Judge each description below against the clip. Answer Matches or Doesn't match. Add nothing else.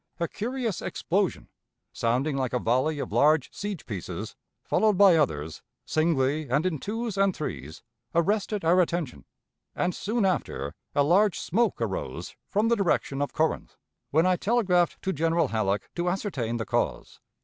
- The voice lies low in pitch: Doesn't match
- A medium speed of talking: Matches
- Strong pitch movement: Matches